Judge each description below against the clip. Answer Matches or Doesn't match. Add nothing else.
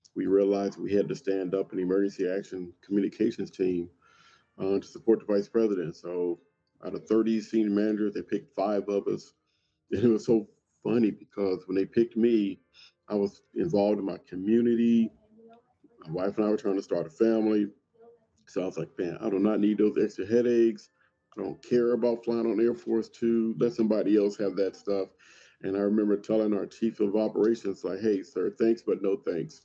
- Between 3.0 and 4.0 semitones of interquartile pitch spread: Doesn't match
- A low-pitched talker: Matches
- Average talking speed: Matches